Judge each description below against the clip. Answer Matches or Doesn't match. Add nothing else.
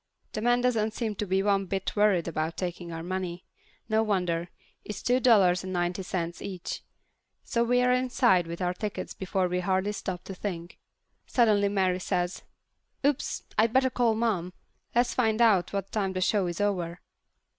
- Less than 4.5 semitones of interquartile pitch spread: Matches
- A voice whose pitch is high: Matches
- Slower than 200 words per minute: Matches